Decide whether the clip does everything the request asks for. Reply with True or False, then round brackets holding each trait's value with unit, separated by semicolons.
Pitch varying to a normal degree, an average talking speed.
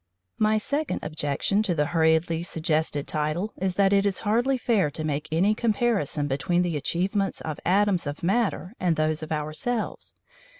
True (5.0 semitones; 165 wpm)